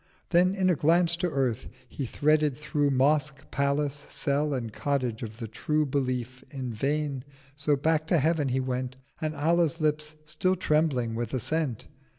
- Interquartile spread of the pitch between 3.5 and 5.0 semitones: No, average, 3.1 semitones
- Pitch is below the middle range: No, medium, 145 Hz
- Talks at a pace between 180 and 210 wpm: No, average, 155 wpm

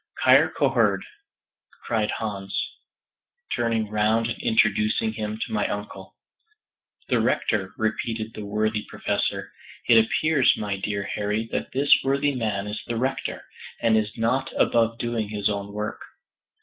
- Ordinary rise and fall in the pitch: No, narrow, 2.1 semitones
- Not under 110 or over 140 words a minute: Yes, slow, 135 wpm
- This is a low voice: Yes, low, 110 Hz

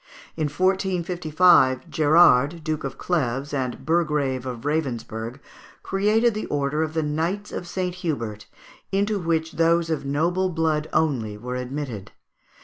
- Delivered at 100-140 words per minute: Yes, slow, 135 wpm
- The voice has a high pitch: No, medium, 155 Hz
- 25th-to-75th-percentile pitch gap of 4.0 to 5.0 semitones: Yes, average, 4.4 semitones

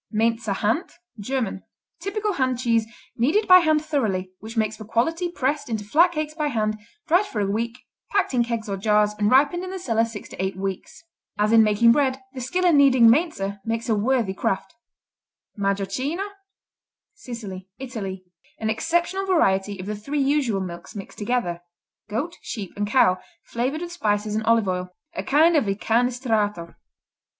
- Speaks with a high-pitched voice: Yes, high, 230 Hz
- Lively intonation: Yes, wide, 6.1 semitones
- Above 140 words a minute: Yes, average, 170 wpm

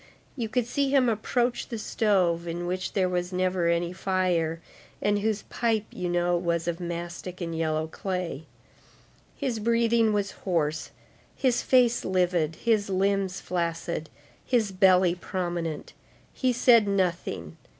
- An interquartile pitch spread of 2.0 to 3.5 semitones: No, average, 4.1 semitones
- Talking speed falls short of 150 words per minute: Yes, average, 140 wpm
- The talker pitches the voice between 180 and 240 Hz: Yes, medium, 185 Hz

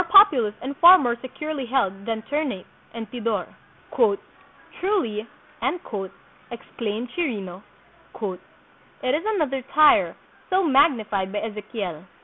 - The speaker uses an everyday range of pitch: No, wide, 6.3 semitones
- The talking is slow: Yes, slow, 105 wpm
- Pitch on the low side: No, very high, 250 Hz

